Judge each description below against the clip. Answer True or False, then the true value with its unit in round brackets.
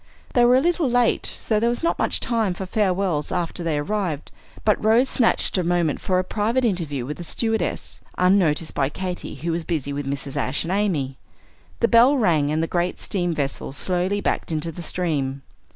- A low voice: False (180 Hz)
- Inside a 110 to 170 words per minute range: False (200 wpm)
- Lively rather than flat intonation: True (5.7 semitones)